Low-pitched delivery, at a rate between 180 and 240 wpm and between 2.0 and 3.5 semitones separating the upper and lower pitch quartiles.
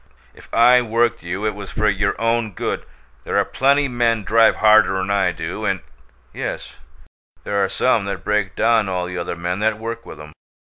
Yes: low, 105 Hz; average, 195 wpm; average, 3.2 semitones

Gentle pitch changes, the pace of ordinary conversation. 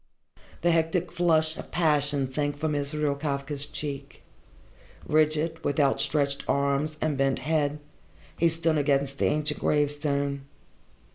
No: narrow, 1.9 semitones; slow, 125 wpm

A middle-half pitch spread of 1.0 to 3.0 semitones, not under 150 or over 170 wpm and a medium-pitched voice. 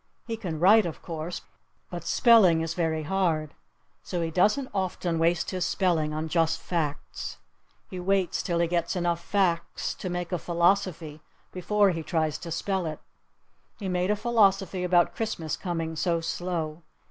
Yes: average, 2.7 semitones; average, 160 wpm; medium, 175 Hz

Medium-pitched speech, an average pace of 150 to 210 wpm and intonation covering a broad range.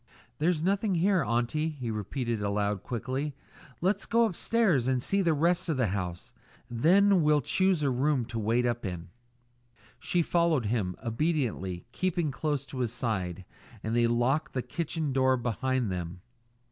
No: low, 130 Hz; average, 160 wpm; wide, 6.2 semitones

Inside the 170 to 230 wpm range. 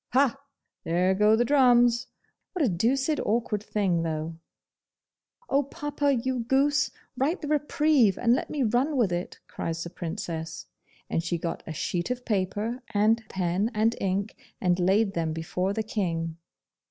No: average, 155 wpm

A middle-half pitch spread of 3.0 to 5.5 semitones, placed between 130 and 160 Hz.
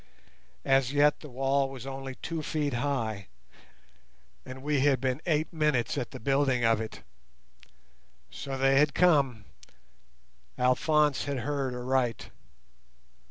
No: narrow, 2.4 semitones; low, 135 Hz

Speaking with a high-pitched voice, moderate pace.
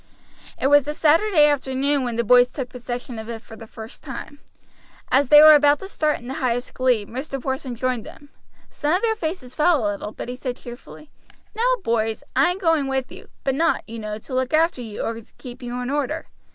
No: very high, 265 Hz; fast, 220 wpm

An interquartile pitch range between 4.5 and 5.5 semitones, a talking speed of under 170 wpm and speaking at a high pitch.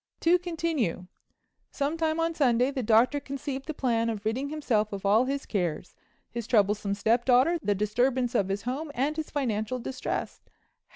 Yes: average, 5.2 semitones; average, 155 wpm; very high, 250 Hz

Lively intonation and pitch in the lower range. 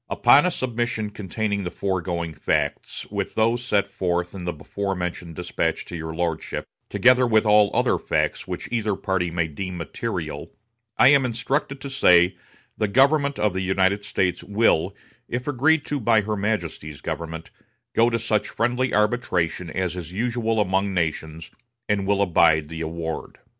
No: average, 5.0 semitones; low, 100 Hz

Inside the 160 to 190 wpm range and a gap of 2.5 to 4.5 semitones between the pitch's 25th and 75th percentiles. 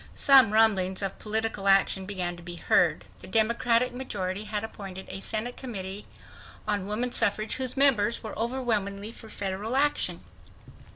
No: average, 150 wpm; average, 3.3 semitones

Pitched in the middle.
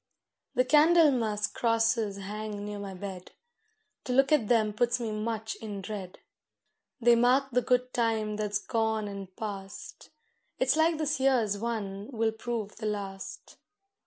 No: high, 220 Hz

